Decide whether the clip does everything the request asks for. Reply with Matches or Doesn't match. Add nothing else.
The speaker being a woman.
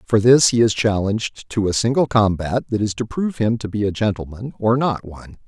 Doesn't match